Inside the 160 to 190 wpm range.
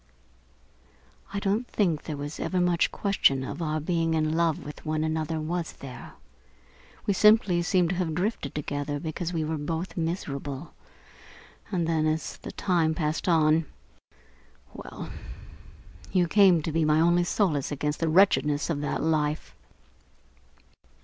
No: average, 145 wpm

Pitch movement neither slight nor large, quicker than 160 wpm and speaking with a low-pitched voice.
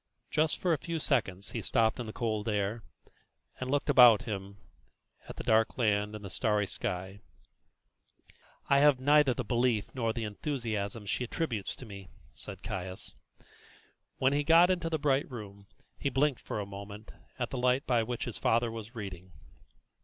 Yes: average, 4.5 semitones; average, 175 wpm; low, 115 Hz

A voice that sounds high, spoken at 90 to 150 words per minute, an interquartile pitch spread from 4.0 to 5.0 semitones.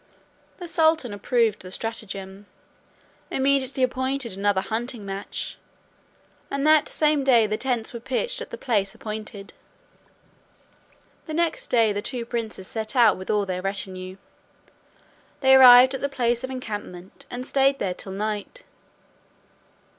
Yes: high, 235 Hz; average, 140 wpm; average, 4.7 semitones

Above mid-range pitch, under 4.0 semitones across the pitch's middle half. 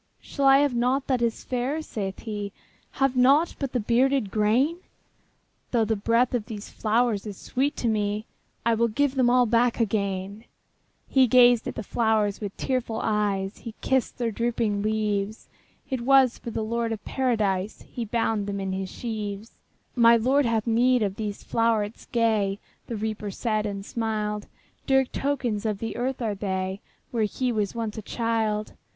Yes: high, 225 Hz; average, 2.8 semitones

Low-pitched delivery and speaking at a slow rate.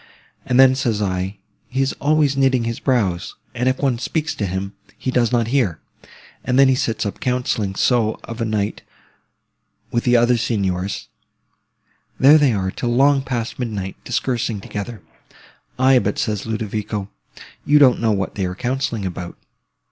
No: low, 115 Hz; average, 165 wpm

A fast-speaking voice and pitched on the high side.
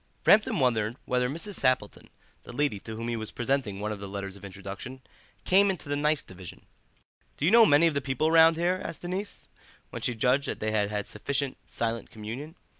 No: fast, 210 wpm; low, 130 Hz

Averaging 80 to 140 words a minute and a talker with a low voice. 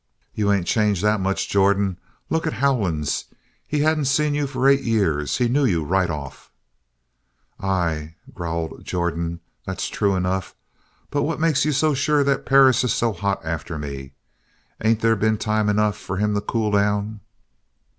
No: average, 165 wpm; low, 105 Hz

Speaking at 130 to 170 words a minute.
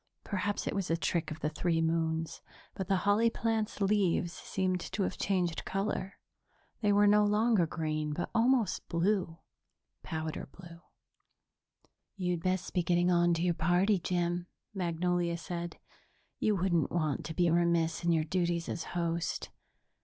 Yes: average, 155 wpm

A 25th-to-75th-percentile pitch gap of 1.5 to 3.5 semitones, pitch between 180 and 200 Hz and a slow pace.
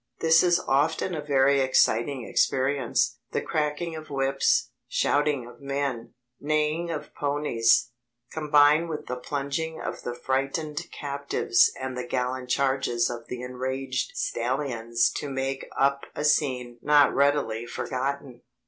No: average, 2.8 semitones; low, 135 Hz; slow, 130 wpm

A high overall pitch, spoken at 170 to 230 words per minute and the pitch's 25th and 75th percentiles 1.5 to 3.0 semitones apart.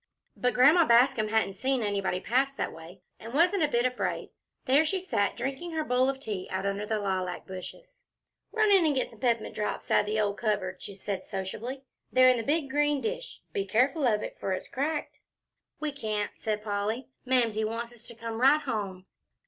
No: high, 235 Hz; average, 200 wpm; average, 5.0 semitones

